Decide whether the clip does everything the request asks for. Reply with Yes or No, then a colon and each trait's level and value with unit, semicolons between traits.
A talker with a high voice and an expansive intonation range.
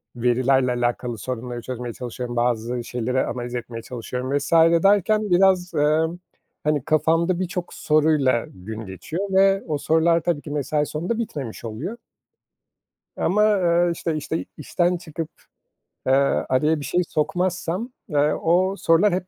No: medium, 155 Hz; wide, 6.0 semitones